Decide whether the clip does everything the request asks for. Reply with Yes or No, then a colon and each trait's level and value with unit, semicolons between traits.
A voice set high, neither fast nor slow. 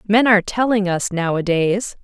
Yes: high, 200 Hz; average, 145 wpm